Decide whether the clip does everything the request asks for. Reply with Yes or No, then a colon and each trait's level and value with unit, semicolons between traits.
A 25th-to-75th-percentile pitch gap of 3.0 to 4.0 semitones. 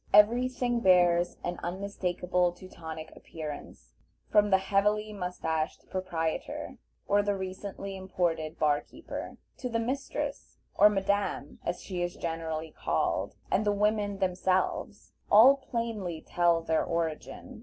Yes: average, 3.5 semitones